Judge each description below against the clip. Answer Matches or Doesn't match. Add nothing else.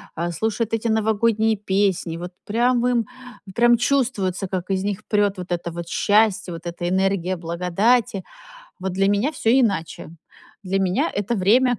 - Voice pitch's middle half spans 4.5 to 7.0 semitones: Doesn't match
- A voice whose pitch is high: Matches